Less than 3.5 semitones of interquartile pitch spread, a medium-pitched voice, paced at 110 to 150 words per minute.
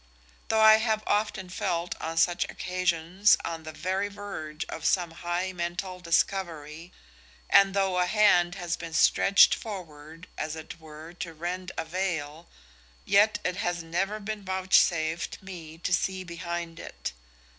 Yes: average, 2.7 semitones; medium, 175 Hz; average, 145 wpm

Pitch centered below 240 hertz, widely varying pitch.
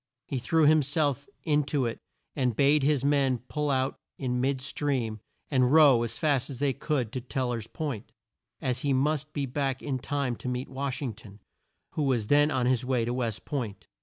No: low, 135 Hz; average, 2.7 semitones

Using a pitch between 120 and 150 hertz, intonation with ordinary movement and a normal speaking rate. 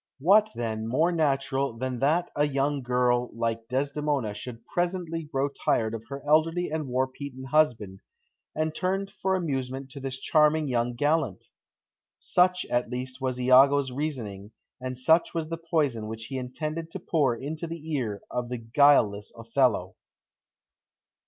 Yes: low, 135 Hz; average, 4.2 semitones; average, 150 wpm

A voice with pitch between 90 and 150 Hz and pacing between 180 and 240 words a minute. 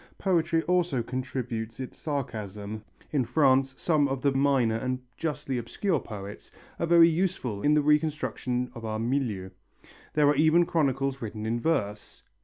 No: low, 135 Hz; average, 150 wpm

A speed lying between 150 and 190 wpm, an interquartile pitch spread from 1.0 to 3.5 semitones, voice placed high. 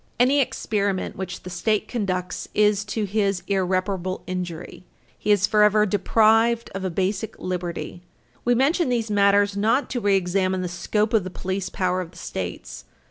Yes: average, 160 wpm; narrow, 2.6 semitones; high, 200 Hz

